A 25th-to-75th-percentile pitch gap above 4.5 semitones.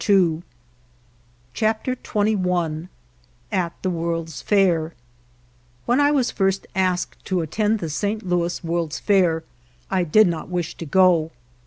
No: average, 3.4 semitones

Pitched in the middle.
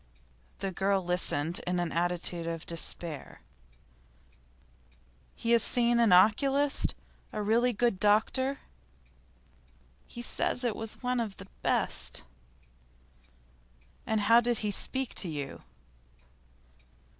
No: high, 210 Hz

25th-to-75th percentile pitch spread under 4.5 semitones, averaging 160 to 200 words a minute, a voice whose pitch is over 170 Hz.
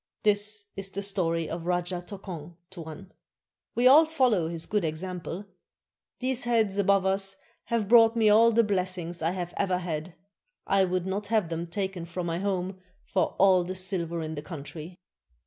Yes: average, 3.0 semitones; average, 170 wpm; medium, 185 Hz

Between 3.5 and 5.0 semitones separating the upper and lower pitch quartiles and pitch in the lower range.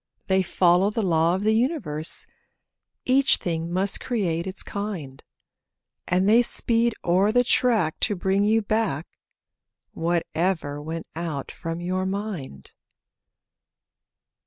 No: average, 4.5 semitones; medium, 185 Hz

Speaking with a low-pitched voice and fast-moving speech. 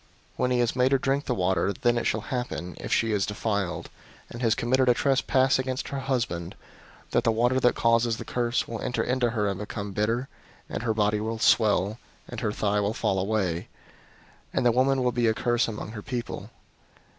Yes: low, 115 Hz; fast, 210 wpm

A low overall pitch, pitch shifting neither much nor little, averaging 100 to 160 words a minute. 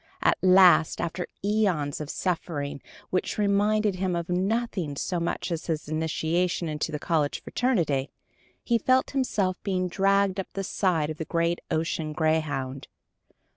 No: medium, 175 Hz; average, 3.9 semitones; average, 145 wpm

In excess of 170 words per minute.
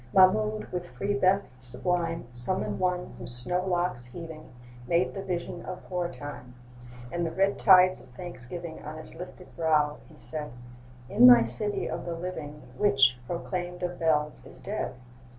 No: average, 160 wpm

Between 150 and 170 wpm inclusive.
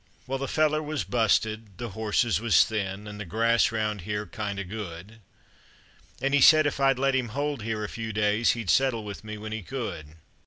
No: fast, 205 wpm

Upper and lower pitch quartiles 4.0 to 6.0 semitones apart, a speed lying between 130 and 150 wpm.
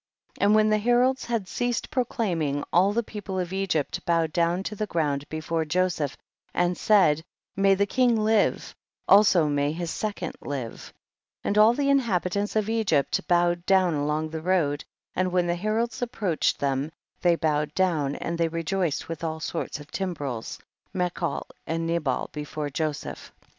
No: average, 4.7 semitones; average, 170 wpm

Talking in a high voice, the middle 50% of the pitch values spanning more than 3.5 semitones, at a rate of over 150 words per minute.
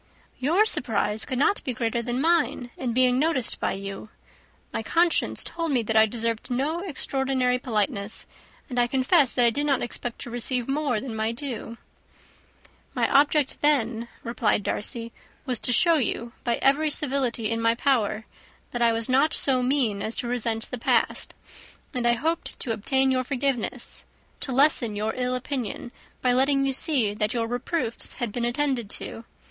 No: very high, 250 Hz; average, 3.1 semitones; average, 175 wpm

